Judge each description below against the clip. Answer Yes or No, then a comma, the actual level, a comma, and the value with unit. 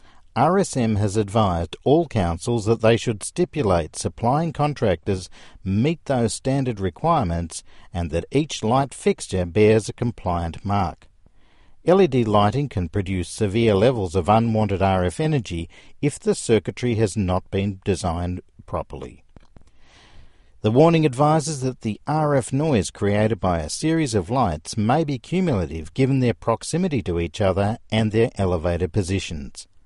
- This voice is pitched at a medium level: No, low, 105 Hz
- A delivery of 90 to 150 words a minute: Yes, slow, 135 wpm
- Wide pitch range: Yes, wide, 6.7 semitones